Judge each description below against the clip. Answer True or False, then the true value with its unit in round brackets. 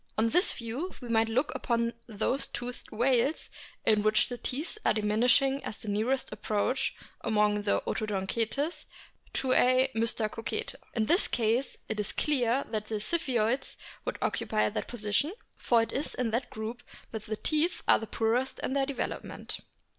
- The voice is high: True (235 Hz)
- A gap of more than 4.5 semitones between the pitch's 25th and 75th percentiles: False (3.4 semitones)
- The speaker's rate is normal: True (160 wpm)